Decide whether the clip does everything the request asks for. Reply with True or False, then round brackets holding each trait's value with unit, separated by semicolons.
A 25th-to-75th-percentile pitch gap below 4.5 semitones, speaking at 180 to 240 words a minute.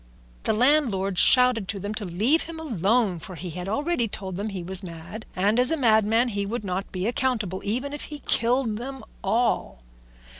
False (4.8 semitones; 195 wpm)